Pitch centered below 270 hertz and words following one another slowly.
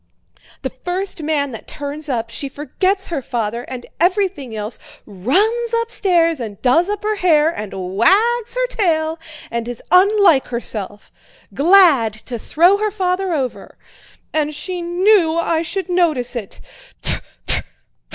No: very high, 320 Hz; slow, 130 wpm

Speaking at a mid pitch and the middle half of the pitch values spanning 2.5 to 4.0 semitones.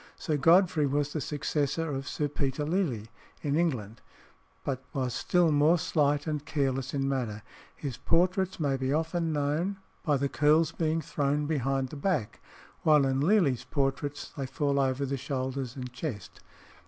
Yes: medium, 145 Hz; average, 2.8 semitones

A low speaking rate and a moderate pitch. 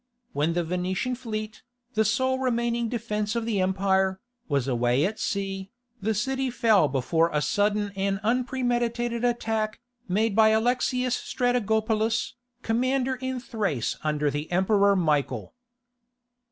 No: slow, 125 wpm; high, 215 Hz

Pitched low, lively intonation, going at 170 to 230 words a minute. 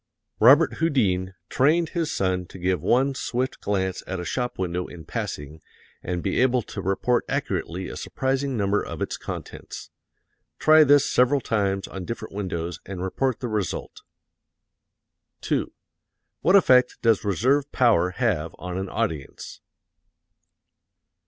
No: low, 105 Hz; wide, 6.1 semitones; average, 140 wpm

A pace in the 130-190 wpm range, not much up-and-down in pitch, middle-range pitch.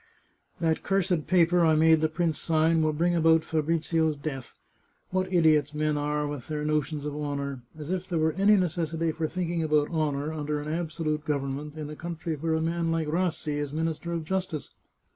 No: average, 200 wpm; narrow, 1.9 semitones; medium, 160 Hz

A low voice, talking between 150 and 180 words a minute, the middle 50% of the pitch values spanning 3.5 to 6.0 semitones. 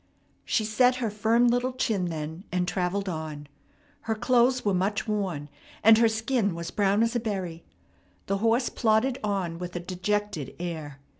No: high, 205 Hz; average, 165 wpm; average, 4.4 semitones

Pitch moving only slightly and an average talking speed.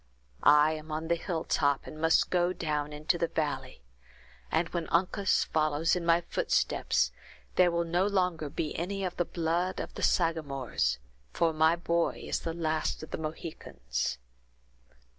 Yes: narrow, 1.9 semitones; average, 160 wpm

